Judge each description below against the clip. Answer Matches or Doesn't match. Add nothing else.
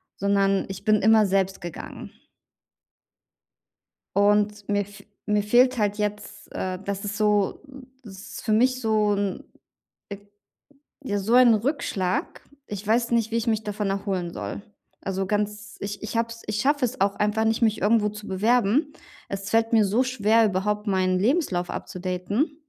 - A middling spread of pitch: Doesn't match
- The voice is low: Doesn't match